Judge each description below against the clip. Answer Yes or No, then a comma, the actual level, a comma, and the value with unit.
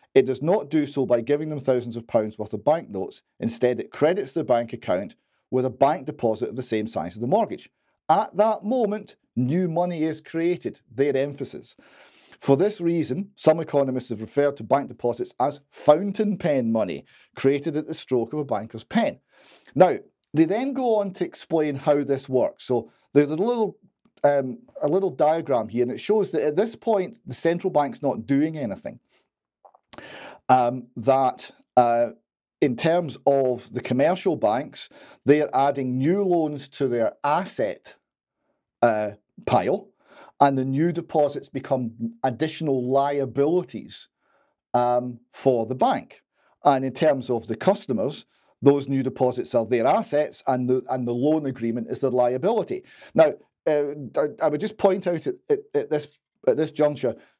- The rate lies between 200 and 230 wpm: No, average, 165 wpm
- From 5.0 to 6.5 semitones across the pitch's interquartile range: No, average, 4.5 semitones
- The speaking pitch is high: No, medium, 145 Hz